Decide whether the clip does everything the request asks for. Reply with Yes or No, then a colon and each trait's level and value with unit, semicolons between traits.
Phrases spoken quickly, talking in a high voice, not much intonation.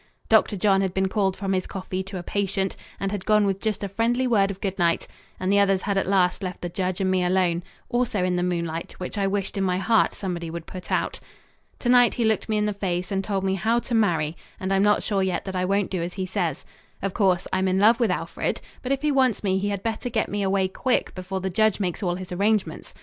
Yes: fast, 260 wpm; high, 195 Hz; narrow, 2.2 semitones